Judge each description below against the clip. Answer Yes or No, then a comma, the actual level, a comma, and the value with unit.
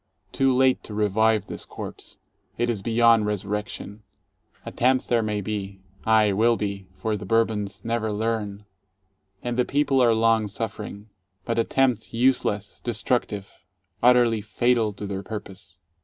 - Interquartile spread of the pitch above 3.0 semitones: No, narrow, 2.4 semitones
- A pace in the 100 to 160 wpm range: Yes, average, 140 wpm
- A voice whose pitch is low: Yes, low, 110 Hz